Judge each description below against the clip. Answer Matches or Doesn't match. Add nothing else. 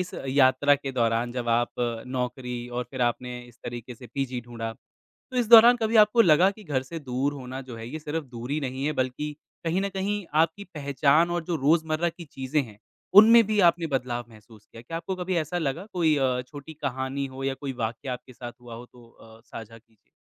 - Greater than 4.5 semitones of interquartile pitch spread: Matches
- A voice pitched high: Doesn't match